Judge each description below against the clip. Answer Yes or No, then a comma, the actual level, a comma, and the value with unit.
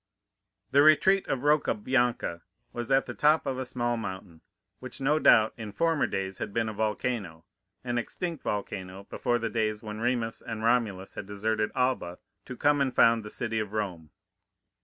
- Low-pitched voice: Yes, low, 115 Hz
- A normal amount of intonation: Yes, average, 3.7 semitones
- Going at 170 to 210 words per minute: Yes, average, 175 wpm